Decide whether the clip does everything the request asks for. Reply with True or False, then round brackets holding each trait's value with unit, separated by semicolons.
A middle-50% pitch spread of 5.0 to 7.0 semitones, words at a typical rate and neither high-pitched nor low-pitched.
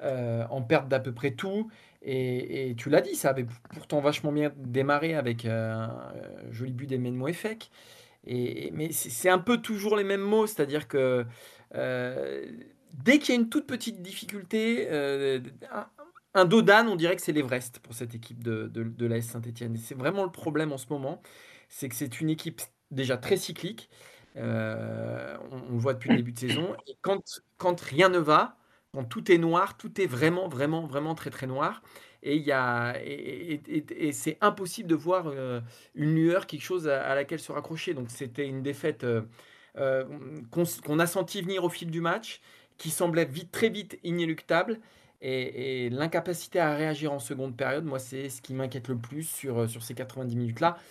True (5.6 semitones; 200 wpm; 145 Hz)